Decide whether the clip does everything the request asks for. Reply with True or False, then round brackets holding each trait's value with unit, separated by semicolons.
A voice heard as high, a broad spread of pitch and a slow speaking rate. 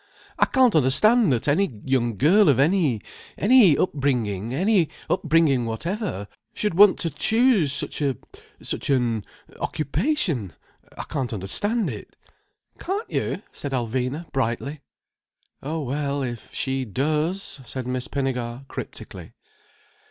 False (140 Hz; 6.5 semitones; 115 wpm)